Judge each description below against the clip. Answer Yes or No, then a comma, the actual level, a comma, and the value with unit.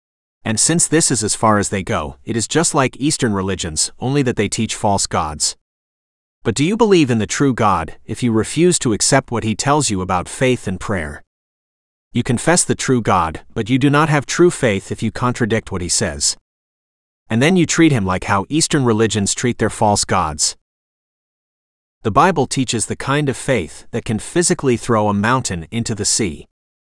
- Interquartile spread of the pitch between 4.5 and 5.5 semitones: Yes, average, 5.1 semitones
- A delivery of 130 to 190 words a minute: No, average, 200 wpm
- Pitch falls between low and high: No, low, 115 Hz